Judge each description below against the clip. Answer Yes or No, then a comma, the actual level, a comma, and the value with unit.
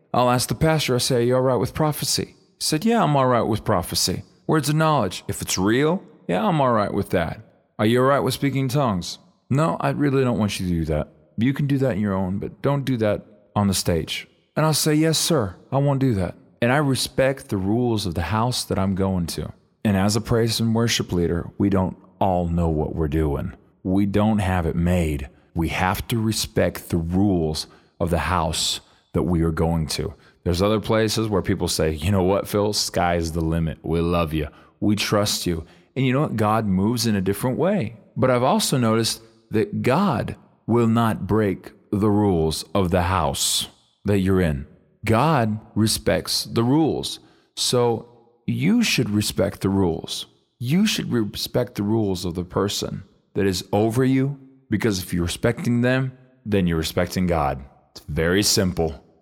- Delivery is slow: No, average, 200 wpm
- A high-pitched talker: No, low, 105 Hz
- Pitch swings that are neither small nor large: No, wide, 5.7 semitones